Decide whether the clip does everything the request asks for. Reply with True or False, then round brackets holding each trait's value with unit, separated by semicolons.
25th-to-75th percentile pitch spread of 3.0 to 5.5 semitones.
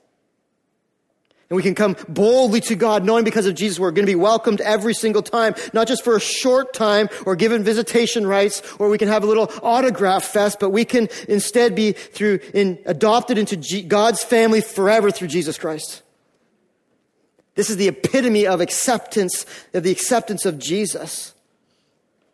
False (2.6 semitones)